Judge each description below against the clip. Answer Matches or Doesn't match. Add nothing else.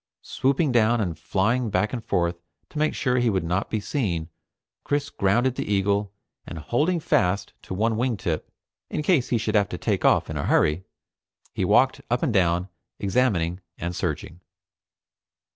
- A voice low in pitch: Matches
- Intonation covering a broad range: Matches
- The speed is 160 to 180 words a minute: Matches